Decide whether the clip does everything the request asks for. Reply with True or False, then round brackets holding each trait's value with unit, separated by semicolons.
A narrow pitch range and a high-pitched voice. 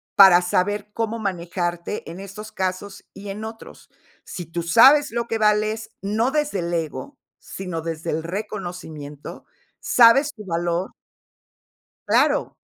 False (4.0 semitones; 195 Hz)